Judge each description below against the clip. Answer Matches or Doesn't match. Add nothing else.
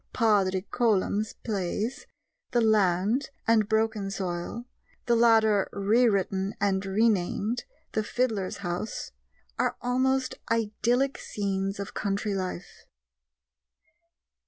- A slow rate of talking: Matches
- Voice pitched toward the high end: Matches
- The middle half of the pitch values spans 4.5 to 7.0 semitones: Doesn't match